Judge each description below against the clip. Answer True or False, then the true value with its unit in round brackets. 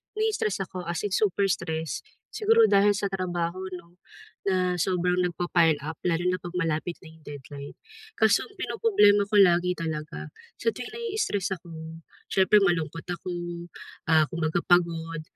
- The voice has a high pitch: False (175 Hz)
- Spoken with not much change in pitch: False (3.2 semitones)